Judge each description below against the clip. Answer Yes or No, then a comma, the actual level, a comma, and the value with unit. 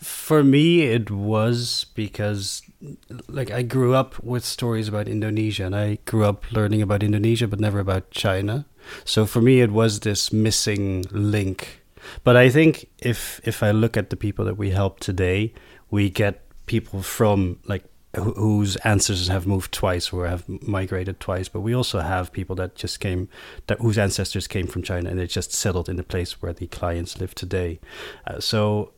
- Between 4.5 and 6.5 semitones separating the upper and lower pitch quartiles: No, average, 3.2 semitones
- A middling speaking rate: Yes, average, 185 wpm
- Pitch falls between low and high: No, low, 105 Hz